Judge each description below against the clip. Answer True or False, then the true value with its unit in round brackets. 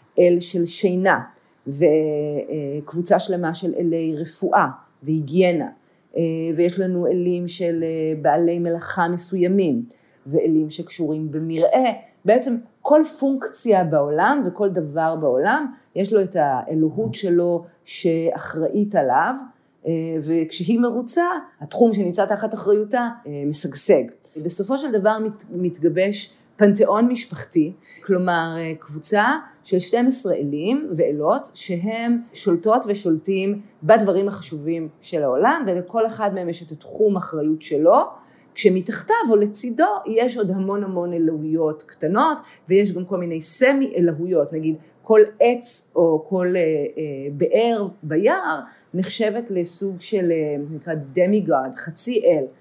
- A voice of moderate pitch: True (180 Hz)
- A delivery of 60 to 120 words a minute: True (110 wpm)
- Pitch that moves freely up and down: False (5.0 semitones)